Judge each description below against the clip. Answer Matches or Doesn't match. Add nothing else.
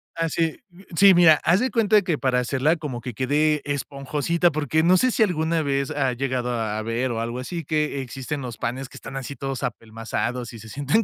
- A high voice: Doesn't match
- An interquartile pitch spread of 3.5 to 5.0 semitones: Matches